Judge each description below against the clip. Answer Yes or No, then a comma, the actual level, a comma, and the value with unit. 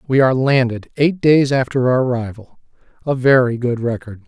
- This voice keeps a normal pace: Yes, average, 155 wpm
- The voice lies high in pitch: No, low, 130 Hz